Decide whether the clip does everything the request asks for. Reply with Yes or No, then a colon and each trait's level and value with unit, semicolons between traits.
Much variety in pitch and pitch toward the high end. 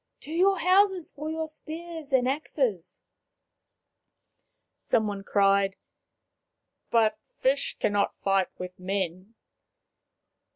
Yes: wide, 8.2 semitones; high, 245 Hz